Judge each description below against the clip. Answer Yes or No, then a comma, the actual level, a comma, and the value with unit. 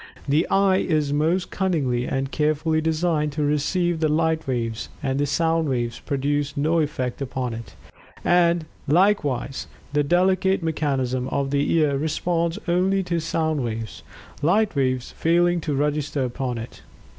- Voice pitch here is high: No, medium, 150 Hz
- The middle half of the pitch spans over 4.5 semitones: No, average, 3.7 semitones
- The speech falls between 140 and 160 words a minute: Yes, average, 145 wpm